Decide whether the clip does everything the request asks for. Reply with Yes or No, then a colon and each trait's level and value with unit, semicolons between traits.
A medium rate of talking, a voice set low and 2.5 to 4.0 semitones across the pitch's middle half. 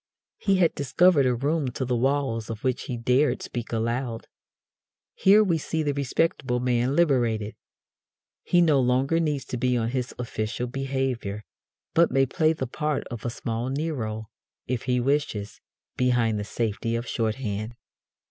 Yes: average, 155 wpm; low, 125 Hz; average, 3.5 semitones